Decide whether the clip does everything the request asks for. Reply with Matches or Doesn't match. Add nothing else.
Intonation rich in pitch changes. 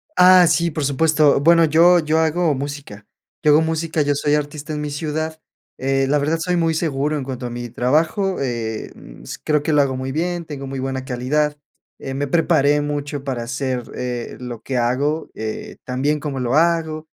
Doesn't match